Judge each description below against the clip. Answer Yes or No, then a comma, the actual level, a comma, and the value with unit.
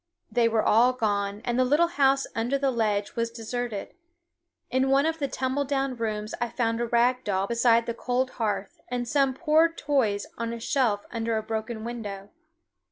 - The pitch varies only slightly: No, average, 3.0 semitones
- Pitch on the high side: Yes, high, 235 Hz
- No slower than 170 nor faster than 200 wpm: Yes, average, 185 wpm